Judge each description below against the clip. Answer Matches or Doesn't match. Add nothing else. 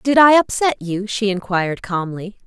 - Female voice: Matches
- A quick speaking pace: Doesn't match